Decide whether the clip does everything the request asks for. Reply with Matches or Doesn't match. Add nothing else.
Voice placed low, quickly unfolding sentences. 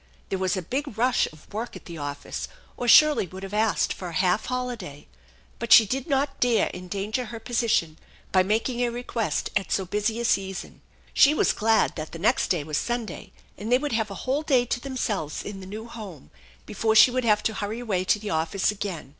Doesn't match